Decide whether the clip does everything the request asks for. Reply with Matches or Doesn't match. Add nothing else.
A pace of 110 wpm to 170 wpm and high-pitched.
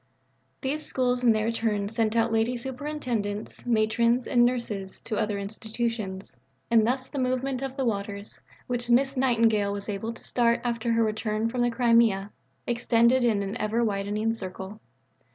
Matches